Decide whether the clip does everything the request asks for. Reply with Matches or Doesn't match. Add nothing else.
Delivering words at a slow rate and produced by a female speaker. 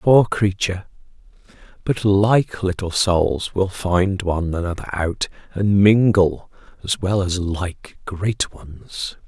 Doesn't match